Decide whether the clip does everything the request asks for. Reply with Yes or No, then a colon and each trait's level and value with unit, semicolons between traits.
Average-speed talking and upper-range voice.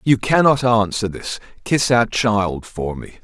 No: average, 165 wpm; low, 110 Hz